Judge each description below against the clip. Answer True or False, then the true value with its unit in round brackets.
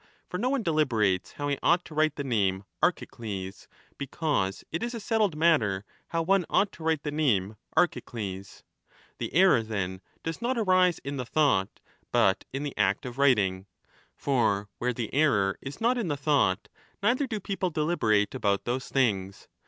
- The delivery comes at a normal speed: True (180 wpm)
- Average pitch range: False (8.5 semitones)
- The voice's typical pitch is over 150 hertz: False (140 Hz)